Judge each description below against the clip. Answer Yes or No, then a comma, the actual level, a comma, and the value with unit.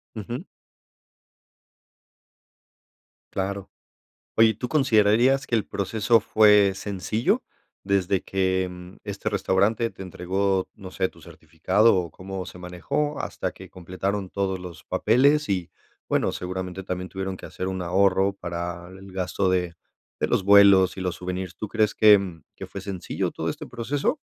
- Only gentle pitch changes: Yes, narrow, 2.2 semitones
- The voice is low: Yes, very low, 95 Hz